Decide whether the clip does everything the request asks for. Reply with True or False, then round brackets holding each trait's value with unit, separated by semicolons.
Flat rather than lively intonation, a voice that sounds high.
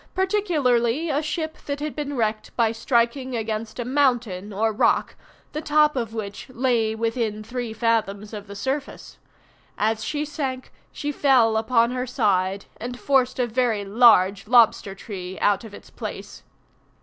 False (3.7 semitones; 235 Hz)